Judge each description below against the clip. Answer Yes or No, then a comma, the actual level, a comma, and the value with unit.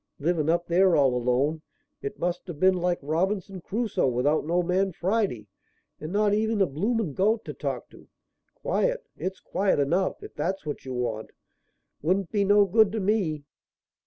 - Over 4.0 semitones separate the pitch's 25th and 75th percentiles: Yes, average, 4.9 semitones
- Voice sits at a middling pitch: Yes, medium, 180 Hz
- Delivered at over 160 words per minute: Yes, average, 170 wpm